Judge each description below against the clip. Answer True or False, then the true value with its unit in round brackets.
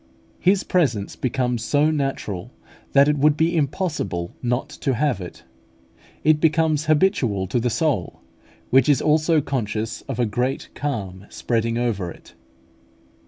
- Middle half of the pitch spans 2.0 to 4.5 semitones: False (5.2 semitones)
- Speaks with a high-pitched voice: False (135 Hz)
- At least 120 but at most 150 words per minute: True (140 wpm)